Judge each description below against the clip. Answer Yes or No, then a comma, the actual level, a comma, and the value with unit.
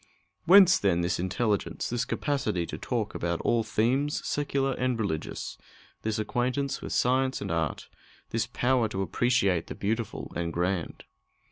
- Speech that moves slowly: No, average, 145 wpm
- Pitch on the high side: No, low, 115 Hz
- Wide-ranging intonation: Yes, wide, 5.7 semitones